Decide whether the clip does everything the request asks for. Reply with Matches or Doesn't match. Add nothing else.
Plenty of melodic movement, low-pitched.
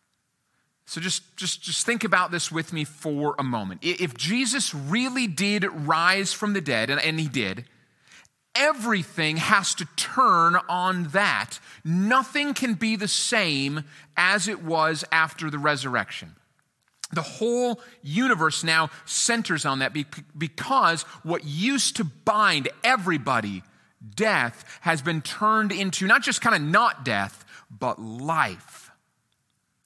Doesn't match